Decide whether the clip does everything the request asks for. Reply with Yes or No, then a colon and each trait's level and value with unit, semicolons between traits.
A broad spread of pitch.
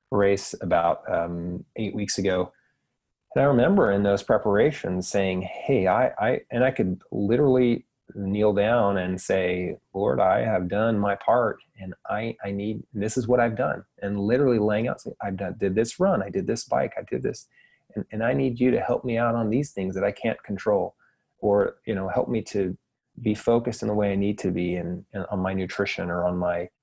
No: average, 3.8 semitones